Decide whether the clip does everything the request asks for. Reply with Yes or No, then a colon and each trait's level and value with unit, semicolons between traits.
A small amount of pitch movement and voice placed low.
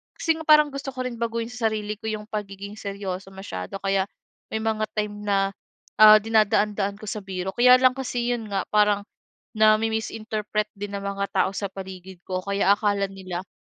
No: narrow, 2.1 semitones; high, 210 Hz